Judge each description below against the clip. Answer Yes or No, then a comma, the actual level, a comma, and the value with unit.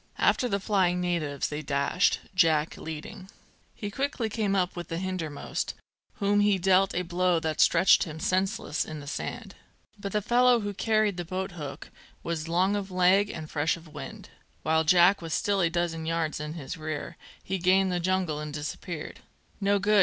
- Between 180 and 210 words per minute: Yes, average, 185 wpm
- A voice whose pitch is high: No, medium, 180 Hz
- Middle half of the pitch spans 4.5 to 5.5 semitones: No, average, 3.6 semitones